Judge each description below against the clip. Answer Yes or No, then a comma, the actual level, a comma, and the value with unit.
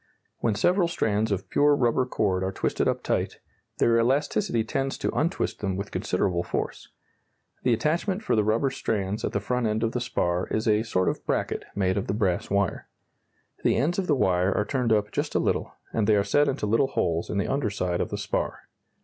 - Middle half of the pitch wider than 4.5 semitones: Yes, average, 5.0 semitones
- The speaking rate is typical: No, fast, 215 wpm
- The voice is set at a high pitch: No, low, 110 Hz